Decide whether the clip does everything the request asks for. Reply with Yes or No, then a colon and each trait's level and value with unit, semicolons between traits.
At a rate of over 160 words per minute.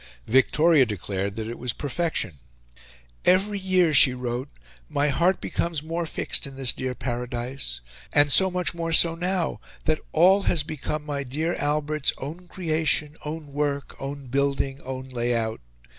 No: average, 155 wpm